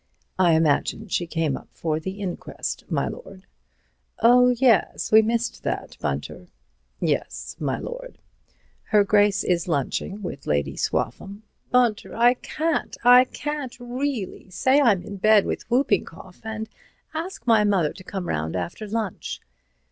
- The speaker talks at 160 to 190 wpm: No, average, 140 wpm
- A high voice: Yes, high, 210 Hz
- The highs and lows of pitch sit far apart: Yes, wide, 5.9 semitones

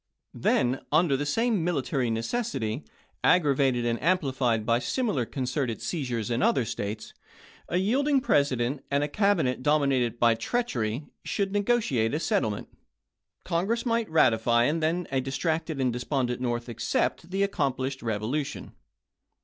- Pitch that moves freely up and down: Yes, wide, 6.3 semitones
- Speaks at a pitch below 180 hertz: Yes, low, 135 Hz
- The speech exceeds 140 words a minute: No, slow, 135 wpm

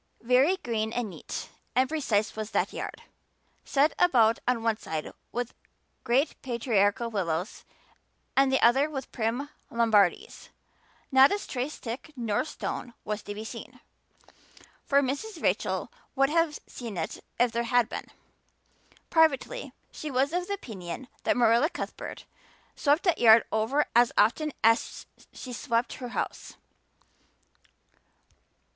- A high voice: Yes, high, 245 Hz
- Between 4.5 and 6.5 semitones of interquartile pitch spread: No, average, 4.0 semitones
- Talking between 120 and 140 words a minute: Yes, slow, 135 wpm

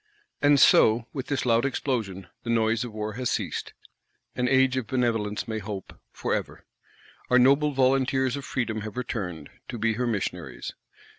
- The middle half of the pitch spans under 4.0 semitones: Yes, average, 3.3 semitones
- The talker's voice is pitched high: No, low, 120 Hz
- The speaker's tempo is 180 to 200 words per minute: No, average, 165 wpm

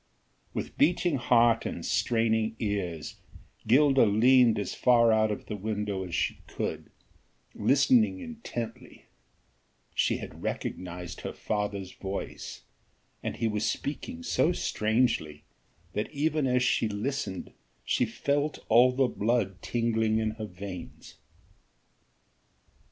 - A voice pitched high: No, low, 115 Hz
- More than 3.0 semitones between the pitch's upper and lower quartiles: Yes, average, 4.0 semitones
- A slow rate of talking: Yes, slow, 120 wpm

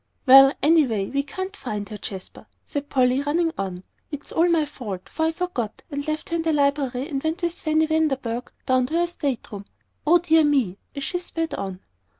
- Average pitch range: Yes, average, 4.5 semitones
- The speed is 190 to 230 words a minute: Yes, fast, 205 wpm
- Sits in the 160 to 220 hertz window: No, very high, 285 Hz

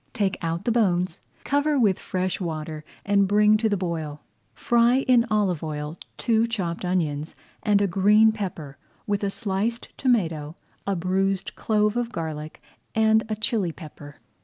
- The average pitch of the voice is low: No, high, 195 Hz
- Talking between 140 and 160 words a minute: Yes, average, 155 wpm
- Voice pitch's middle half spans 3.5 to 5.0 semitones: Yes, average, 4.7 semitones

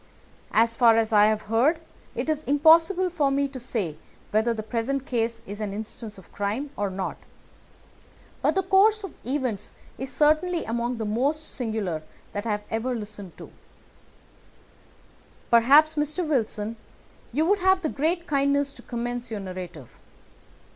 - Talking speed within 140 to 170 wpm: Yes, average, 155 wpm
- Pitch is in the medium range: No, high, 240 Hz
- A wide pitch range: Yes, wide, 5.8 semitones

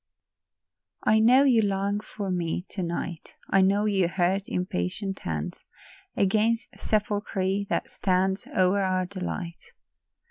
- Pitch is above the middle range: Yes, high, 195 Hz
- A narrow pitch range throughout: Yes, narrow, 2.2 semitones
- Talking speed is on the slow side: Yes, slow, 130 wpm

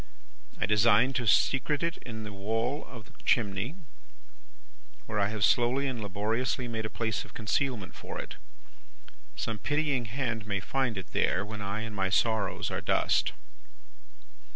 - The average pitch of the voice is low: Yes, low, 110 Hz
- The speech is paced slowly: No, average, 155 wpm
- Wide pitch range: No, average, 3.5 semitones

